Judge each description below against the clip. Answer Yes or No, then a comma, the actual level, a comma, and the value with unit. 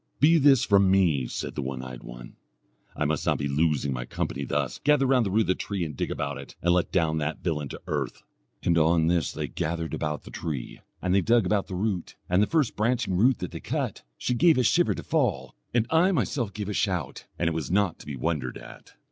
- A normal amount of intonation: No, wide, 6.5 semitones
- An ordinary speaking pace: No, fast, 240 wpm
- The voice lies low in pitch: Yes, very low, 90 Hz